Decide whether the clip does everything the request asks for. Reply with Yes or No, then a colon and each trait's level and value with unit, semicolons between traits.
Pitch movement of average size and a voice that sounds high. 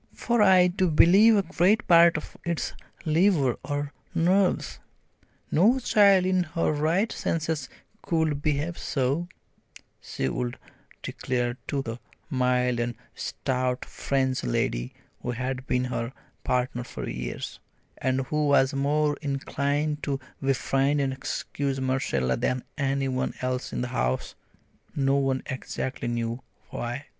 No: average, 4.2 semitones; medium, 140 Hz